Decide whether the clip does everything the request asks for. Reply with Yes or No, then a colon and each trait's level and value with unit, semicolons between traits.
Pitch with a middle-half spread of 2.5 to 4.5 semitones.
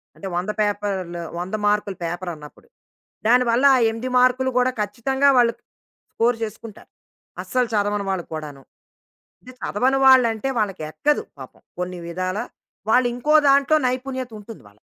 No: average, 5.1 semitones